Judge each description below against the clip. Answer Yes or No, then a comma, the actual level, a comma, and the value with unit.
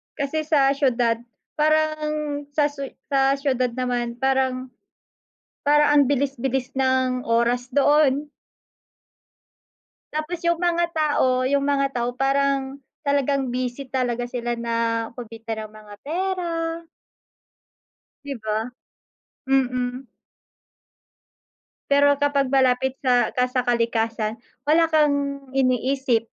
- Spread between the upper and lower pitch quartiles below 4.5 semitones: Yes, narrow, 2.6 semitones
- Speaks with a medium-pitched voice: No, very high, 270 Hz